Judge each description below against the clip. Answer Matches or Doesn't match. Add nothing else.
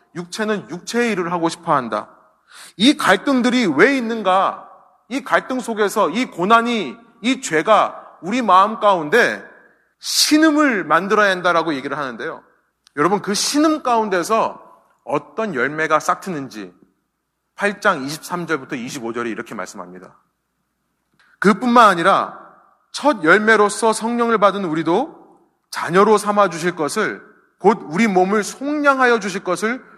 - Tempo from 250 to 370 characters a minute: Matches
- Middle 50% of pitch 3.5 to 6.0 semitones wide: Matches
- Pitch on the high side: Matches